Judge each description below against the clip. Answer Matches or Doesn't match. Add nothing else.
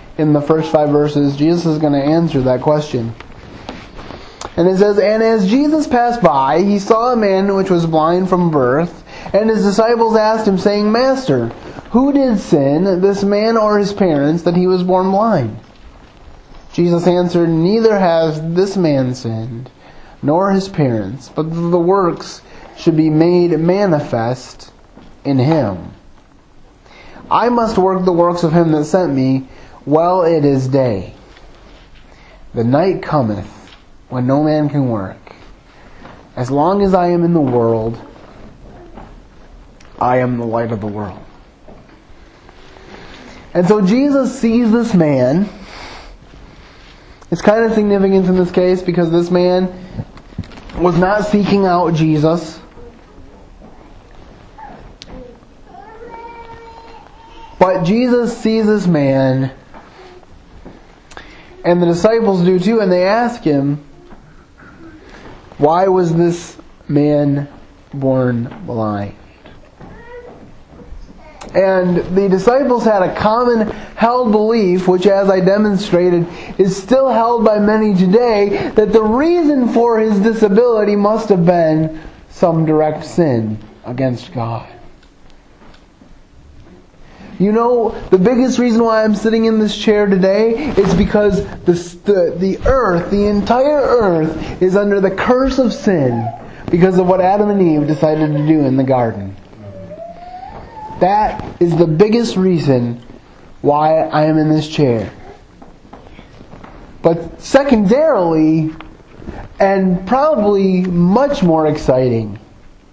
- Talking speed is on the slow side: Matches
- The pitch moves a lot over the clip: Matches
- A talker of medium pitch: Matches